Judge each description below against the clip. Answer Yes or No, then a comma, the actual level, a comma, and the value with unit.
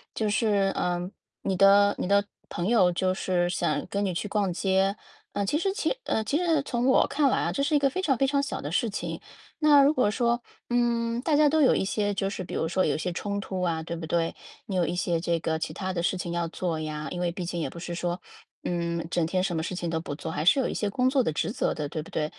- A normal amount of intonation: No, wide, 5.7 semitones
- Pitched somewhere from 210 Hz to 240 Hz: No, high, 190 Hz